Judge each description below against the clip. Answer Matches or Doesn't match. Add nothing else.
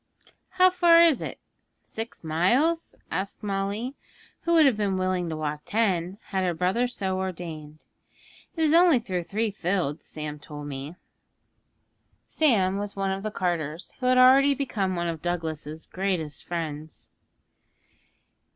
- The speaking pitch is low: Doesn't match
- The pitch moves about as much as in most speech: Doesn't match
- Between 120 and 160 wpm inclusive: Matches